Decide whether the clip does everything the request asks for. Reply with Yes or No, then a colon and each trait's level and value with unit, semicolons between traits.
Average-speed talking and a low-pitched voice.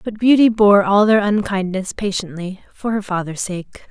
No: average, 170 wpm; high, 200 Hz